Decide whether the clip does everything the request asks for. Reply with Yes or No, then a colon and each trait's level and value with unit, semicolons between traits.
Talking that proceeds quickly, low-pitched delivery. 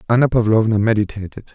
No: slow, 115 wpm; low, 110 Hz